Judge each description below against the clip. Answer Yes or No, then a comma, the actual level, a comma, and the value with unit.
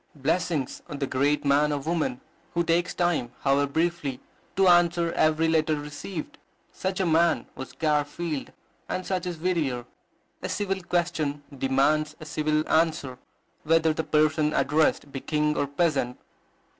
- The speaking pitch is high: No, medium, 155 Hz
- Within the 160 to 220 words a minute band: No, average, 145 wpm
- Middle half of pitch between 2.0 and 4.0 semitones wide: Yes, average, 2.9 semitones